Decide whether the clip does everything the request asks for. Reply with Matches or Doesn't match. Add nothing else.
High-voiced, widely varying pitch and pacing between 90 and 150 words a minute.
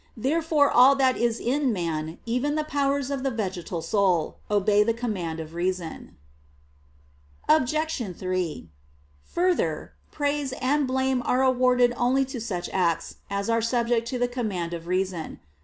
Matches